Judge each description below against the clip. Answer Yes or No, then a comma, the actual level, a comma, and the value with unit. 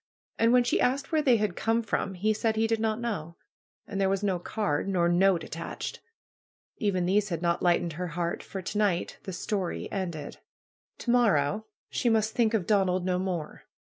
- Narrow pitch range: No, average, 3.9 semitones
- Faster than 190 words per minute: Yes, average, 200 wpm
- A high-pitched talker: Yes, high, 195 Hz